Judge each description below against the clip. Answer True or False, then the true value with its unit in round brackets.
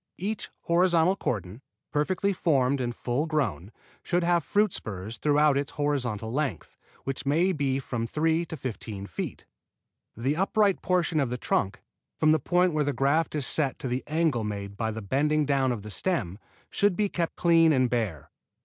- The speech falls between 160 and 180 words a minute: True (175 wpm)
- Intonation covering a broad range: True (5.7 semitones)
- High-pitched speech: False (145 Hz)